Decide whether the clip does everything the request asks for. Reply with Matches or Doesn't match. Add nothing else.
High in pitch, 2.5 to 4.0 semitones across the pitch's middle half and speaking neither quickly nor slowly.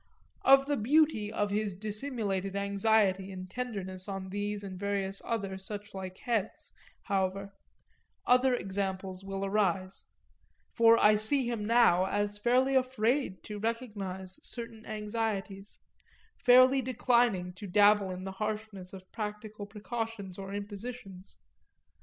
Doesn't match